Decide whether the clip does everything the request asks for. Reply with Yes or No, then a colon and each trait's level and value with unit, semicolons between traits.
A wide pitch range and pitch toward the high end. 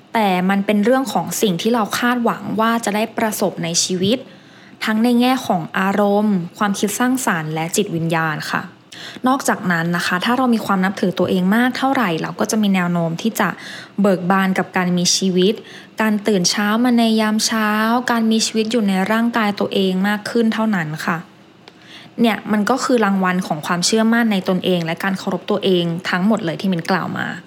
No: average, 3.6 semitones; high, 205 Hz